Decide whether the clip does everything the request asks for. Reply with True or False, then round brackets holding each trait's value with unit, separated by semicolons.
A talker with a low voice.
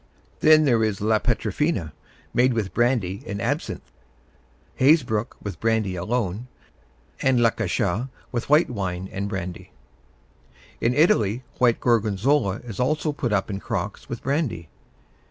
True (115 Hz)